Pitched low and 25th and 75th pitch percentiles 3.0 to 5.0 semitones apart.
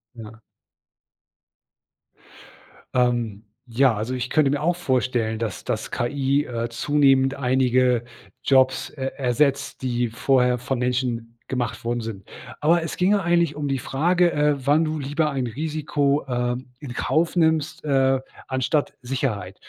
Yes: low, 130 Hz; average, 3.4 semitones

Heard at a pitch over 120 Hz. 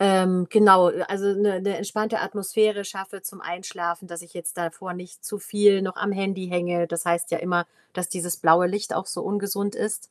Yes: high, 190 Hz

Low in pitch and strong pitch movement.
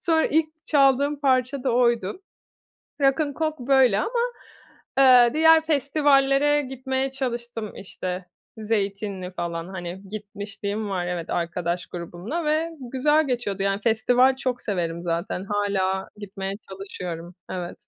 No: high, 230 Hz; wide, 6.2 semitones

